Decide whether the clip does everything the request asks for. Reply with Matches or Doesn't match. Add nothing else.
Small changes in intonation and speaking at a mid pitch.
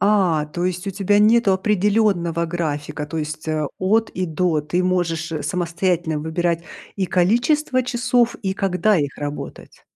Doesn't match